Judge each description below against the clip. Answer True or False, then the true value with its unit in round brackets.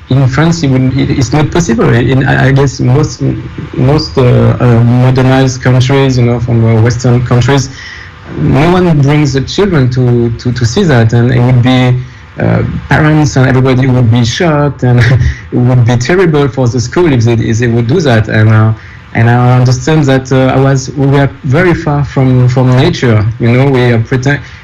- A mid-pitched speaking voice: False (130 Hz)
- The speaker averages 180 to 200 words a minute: True (190 wpm)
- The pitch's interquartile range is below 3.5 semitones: True (2.4 semitones)